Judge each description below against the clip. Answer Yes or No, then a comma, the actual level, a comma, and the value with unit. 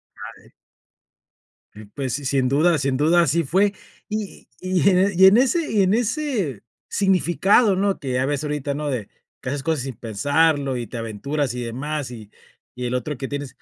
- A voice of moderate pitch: Yes, medium, 145 Hz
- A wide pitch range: Yes, wide, 6.3 semitones